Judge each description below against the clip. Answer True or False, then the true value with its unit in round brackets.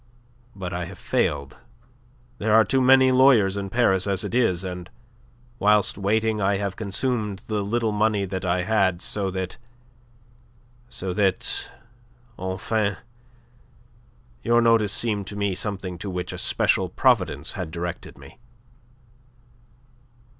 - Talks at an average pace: False (130 wpm)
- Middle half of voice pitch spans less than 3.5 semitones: True (2.9 semitones)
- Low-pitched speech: True (100 Hz)